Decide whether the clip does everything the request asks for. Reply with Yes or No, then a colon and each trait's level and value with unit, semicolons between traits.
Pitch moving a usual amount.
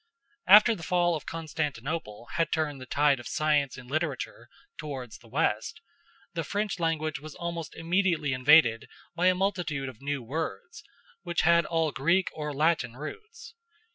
Yes: average, 3.7 semitones